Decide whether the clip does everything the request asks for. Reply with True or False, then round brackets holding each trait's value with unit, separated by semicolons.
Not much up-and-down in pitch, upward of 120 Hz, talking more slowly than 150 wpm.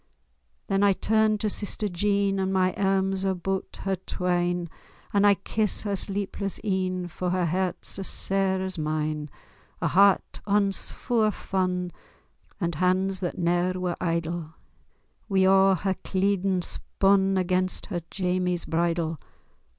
True (1.7 semitones; 190 Hz; 140 wpm)